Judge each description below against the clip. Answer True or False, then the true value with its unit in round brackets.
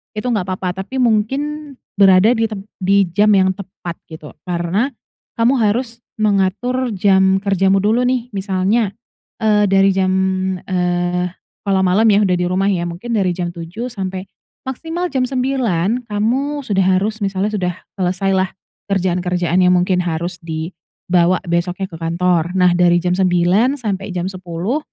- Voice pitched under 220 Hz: True (190 Hz)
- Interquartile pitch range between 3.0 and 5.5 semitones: True (3.4 semitones)